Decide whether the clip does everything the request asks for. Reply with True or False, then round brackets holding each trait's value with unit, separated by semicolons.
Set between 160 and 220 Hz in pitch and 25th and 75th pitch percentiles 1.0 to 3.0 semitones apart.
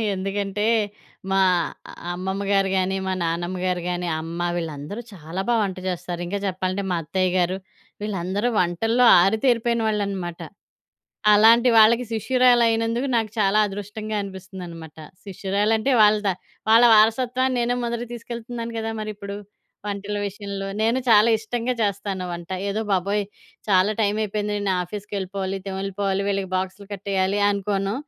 True (200 Hz; 2.7 semitones)